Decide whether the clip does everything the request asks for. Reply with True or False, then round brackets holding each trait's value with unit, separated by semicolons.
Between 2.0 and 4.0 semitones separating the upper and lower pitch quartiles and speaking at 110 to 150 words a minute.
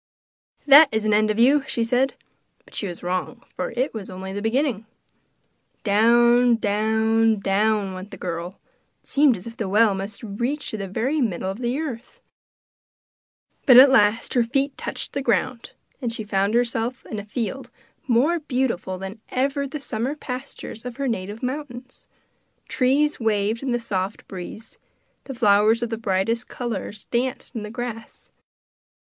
False (3.6 semitones; 165 wpm)